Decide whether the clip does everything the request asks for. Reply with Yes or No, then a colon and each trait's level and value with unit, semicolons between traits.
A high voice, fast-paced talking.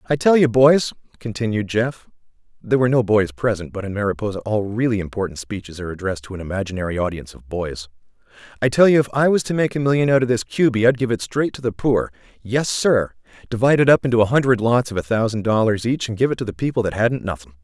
No: low, 115 Hz; fast, 230 wpm